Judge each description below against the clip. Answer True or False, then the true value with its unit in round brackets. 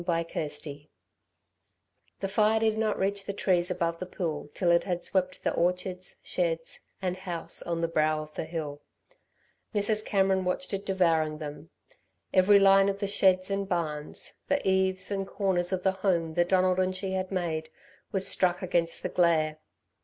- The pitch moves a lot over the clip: False (2.6 semitones)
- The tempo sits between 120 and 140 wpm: False (175 wpm)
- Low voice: False (185 Hz)